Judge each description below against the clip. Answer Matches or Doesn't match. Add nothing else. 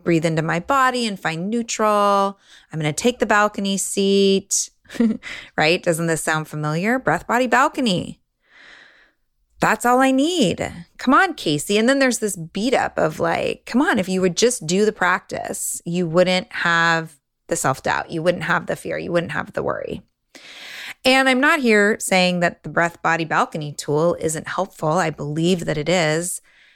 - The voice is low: Doesn't match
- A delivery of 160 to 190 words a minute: Matches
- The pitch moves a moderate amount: Doesn't match